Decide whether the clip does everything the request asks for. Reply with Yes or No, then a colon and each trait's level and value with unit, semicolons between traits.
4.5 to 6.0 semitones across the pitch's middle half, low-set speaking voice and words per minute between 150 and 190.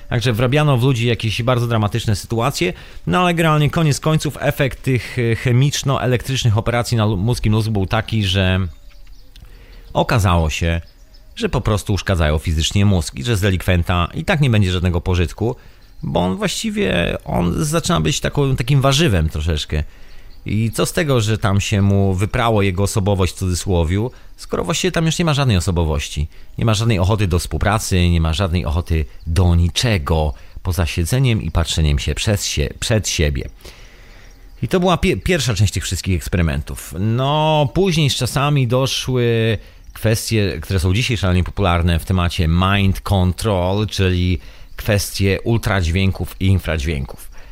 Yes: wide, 5.6 semitones; low, 100 Hz; average, 155 wpm